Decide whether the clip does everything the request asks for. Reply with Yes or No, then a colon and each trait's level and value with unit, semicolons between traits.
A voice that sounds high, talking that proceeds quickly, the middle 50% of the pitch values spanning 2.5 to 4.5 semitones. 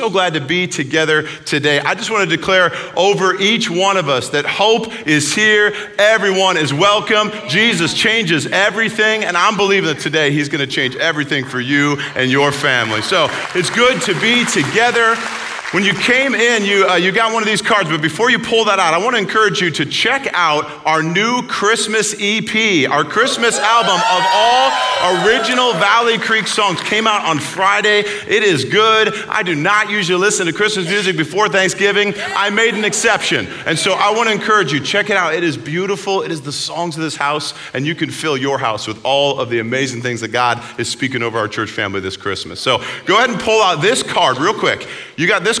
No: high, 195 Hz; fast, 215 wpm; wide, 5.6 semitones